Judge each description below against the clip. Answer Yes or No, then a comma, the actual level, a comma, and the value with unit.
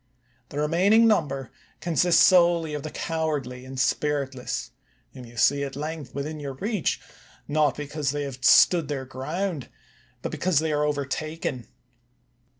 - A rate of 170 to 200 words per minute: No, average, 145 wpm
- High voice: No, medium, 150 Hz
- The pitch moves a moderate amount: Yes, average, 3.2 semitones